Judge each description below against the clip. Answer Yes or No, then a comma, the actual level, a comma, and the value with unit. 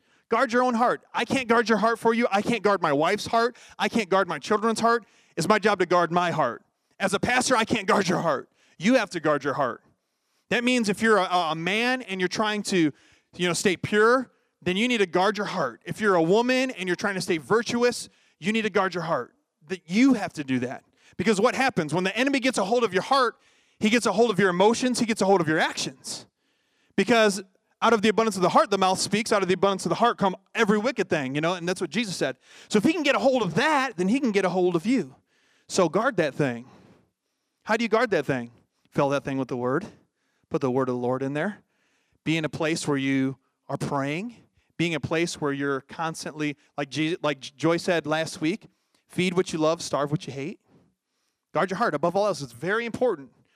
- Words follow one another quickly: Yes, fast, 250 wpm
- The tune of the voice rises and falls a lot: Yes, wide, 6.0 semitones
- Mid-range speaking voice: No, high, 195 Hz